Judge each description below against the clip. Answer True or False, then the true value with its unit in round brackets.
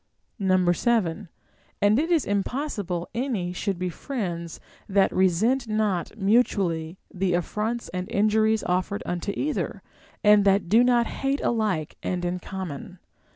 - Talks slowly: True (130 wpm)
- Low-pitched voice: False (200 Hz)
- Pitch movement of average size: True (4.0 semitones)